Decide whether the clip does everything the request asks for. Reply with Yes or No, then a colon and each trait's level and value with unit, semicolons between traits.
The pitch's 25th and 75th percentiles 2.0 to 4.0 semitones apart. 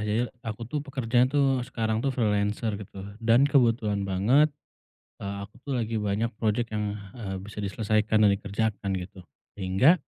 Yes: average, 2.8 semitones